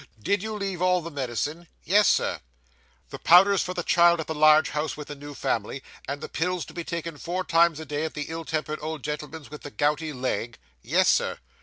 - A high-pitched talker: No, medium, 160 Hz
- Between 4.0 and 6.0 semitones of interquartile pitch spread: No, average, 2.7 semitones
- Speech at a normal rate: No, fast, 220 wpm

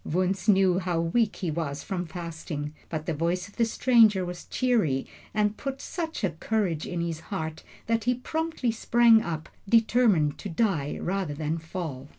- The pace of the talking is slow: No, average, 170 wpm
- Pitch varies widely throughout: Yes, wide, 5.7 semitones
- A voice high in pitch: No, medium, 180 Hz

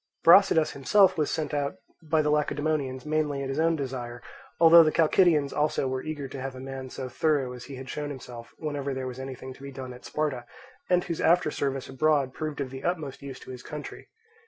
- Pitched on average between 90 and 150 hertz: Yes, medium, 140 Hz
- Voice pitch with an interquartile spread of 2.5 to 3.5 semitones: Yes, average, 2.8 semitones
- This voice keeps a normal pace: No, fast, 215 wpm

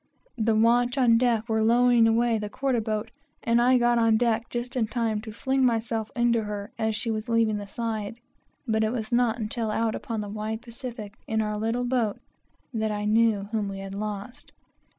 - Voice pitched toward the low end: No, high, 225 Hz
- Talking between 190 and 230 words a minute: Yes, average, 200 wpm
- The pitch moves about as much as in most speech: No, narrow, 1.8 semitones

